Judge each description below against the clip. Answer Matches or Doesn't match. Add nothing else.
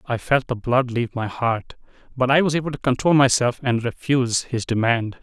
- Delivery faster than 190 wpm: Matches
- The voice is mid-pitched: Doesn't match